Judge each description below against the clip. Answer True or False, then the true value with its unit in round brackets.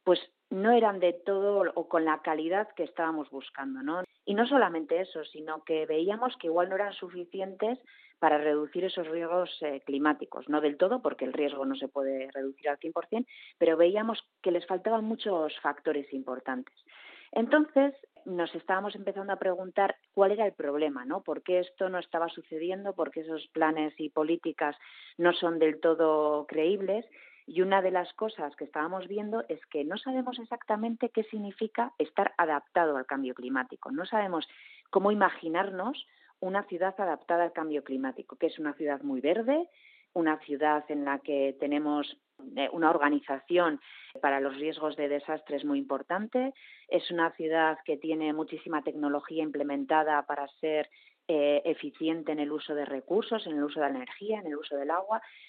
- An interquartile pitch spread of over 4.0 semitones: True (4.8 semitones)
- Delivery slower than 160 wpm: False (175 wpm)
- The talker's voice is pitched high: False (165 Hz)